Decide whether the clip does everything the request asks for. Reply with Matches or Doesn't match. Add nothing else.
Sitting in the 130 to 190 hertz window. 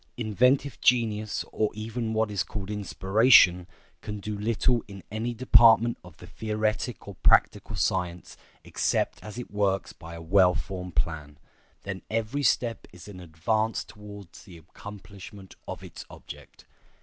Doesn't match